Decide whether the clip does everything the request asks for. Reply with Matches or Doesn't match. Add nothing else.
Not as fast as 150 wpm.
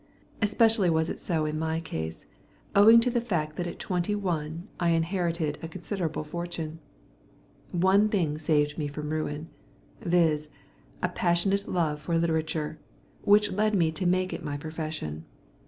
Doesn't match